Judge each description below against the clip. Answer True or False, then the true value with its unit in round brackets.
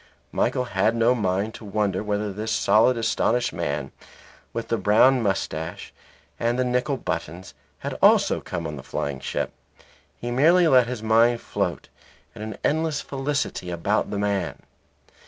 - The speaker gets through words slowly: False (155 wpm)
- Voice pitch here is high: False (110 Hz)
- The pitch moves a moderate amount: True (4.3 semitones)